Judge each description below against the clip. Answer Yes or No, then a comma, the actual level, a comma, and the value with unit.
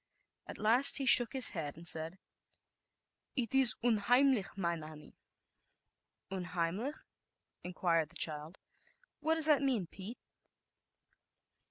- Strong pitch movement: Yes, wide, 7.3 semitones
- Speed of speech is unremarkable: No, slow, 115 wpm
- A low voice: No, high, 195 Hz